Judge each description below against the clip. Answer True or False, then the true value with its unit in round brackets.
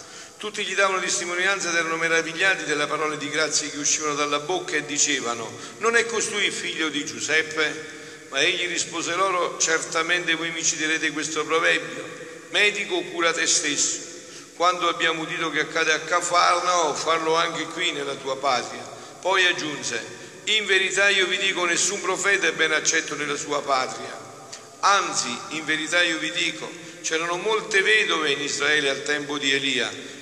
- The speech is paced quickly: False (160 wpm)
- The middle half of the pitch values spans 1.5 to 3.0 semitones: True (2.4 semitones)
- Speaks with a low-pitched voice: False (165 Hz)